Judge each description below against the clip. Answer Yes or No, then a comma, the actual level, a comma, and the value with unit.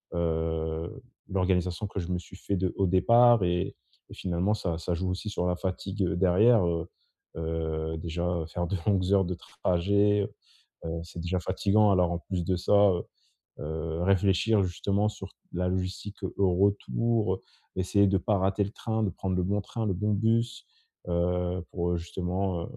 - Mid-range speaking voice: No, very low, 95 Hz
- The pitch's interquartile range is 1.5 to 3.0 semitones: Yes, narrow, 2.6 semitones